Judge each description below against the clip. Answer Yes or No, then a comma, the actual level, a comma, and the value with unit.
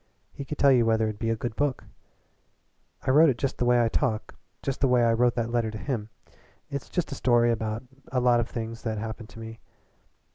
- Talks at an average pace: No, fast, 230 wpm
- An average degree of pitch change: No, narrow, 2.3 semitones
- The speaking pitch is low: Yes, low, 120 Hz